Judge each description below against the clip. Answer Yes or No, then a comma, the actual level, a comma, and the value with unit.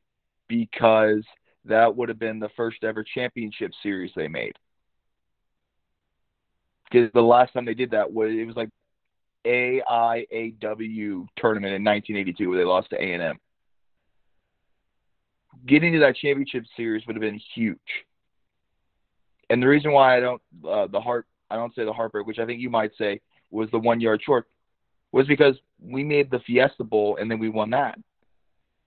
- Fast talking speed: No, average, 165 wpm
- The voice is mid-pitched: No, low, 115 Hz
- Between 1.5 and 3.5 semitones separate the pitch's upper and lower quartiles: Yes, narrow, 2.6 semitones